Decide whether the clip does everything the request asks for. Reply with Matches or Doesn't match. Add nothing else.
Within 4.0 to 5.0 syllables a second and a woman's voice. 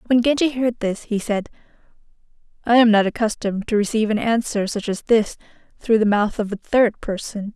Doesn't match